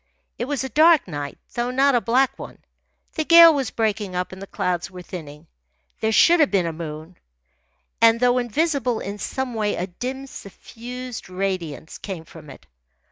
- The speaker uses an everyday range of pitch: No, wide, 6.3 semitones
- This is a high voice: Yes, high, 220 Hz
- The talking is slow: No, average, 180 wpm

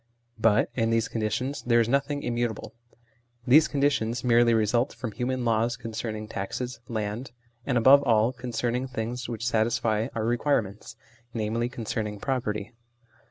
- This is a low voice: Yes, low, 115 Hz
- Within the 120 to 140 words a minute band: Yes, slow, 135 wpm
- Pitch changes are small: Yes, narrow, 2.1 semitones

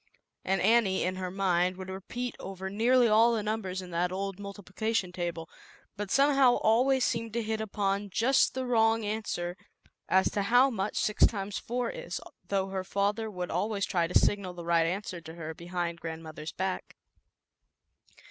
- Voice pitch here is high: Yes, high, 195 Hz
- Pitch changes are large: No, average, 3.6 semitones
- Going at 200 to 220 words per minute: No, average, 175 wpm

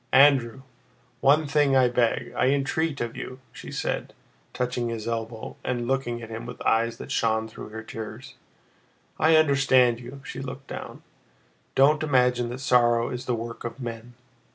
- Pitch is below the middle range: Yes, low, 125 Hz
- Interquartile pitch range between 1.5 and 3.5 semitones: Yes, narrow, 2.6 semitones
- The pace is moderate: Yes, average, 165 wpm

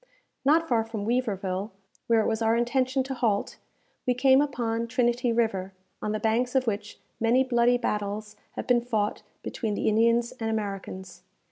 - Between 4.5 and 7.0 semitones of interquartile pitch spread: No, average, 2.7 semitones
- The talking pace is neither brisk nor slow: Yes, average, 165 wpm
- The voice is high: Yes, high, 230 Hz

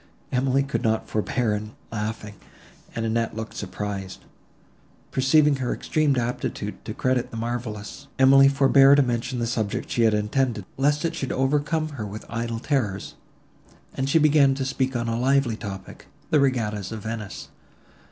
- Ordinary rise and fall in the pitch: Yes, average, 3.7 semitones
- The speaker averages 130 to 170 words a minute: Yes, average, 150 wpm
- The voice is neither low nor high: No, low, 120 Hz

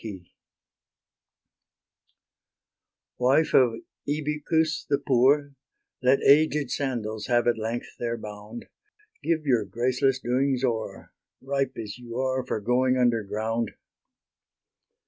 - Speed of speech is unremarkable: No, slow, 100 wpm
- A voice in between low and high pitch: No, low, 125 Hz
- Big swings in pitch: No, average, 3.2 semitones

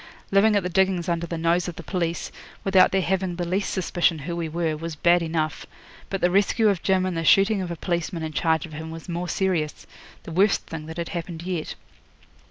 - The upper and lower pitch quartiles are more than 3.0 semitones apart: No, narrow, 2.4 semitones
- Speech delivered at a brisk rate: Yes, fast, 225 wpm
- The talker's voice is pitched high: No, medium, 175 Hz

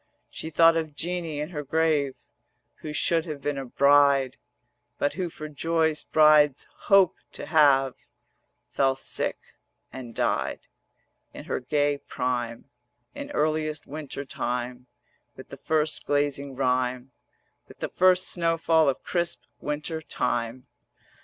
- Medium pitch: Yes, medium, 145 Hz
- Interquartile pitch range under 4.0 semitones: Yes, average, 3.0 semitones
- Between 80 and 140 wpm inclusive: Yes, slow, 135 wpm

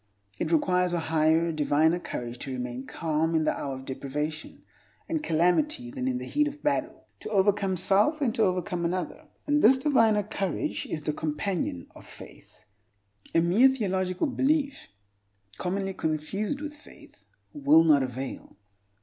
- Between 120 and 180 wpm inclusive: Yes, average, 155 wpm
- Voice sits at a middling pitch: Yes, medium, 180 Hz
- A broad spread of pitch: Yes, wide, 7.9 semitones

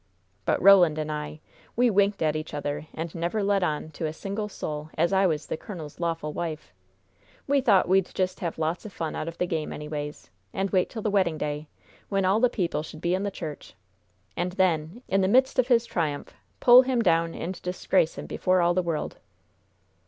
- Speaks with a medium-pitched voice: Yes, medium, 175 Hz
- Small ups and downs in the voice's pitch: No, average, 3.9 semitones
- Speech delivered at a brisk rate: Yes, fast, 210 wpm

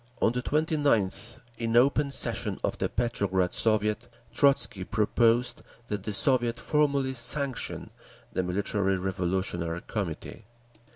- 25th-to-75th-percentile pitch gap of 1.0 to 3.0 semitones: No, average, 5.3 semitones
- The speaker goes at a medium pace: No, slow, 115 wpm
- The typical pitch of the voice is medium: No, low, 115 Hz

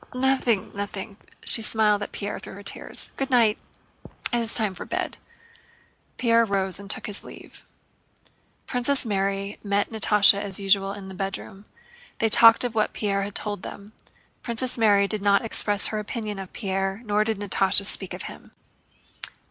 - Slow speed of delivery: No, average, 170 wpm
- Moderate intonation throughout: No, narrow, 2.2 semitones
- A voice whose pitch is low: No, high, 205 Hz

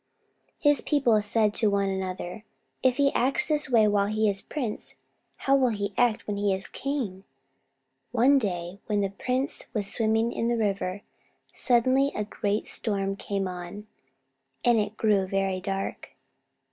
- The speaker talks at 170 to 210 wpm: No, average, 160 wpm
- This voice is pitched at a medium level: No, high, 210 Hz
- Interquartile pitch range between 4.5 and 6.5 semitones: No, average, 3.6 semitones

